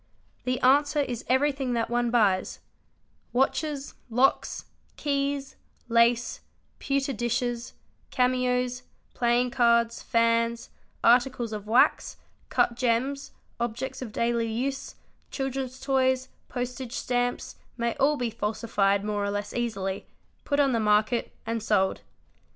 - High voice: Yes, high, 240 Hz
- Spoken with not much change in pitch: Yes, narrow, 2.2 semitones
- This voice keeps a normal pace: No, slow, 120 wpm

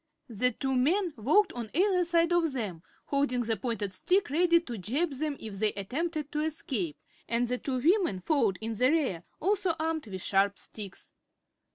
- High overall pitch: Yes, very high, 265 Hz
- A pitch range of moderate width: No, wide, 7.2 semitones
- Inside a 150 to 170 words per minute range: No, average, 180 wpm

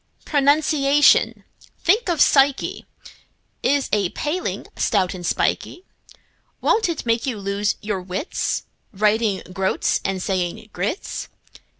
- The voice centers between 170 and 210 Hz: No, high, 220 Hz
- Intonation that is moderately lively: No, wide, 7.1 semitones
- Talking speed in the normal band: No, slow, 105 wpm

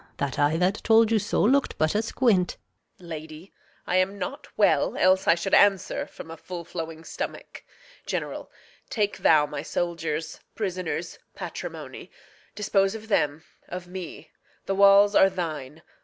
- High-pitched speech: No, medium, 180 Hz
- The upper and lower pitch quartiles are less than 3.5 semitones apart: No, average, 3.8 semitones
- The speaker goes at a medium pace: Yes, average, 150 wpm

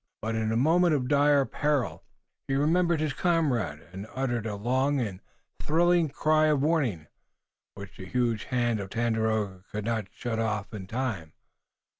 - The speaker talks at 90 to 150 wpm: No, average, 160 wpm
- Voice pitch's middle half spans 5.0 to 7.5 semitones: Yes, wide, 5.6 semitones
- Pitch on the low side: Yes, low, 120 Hz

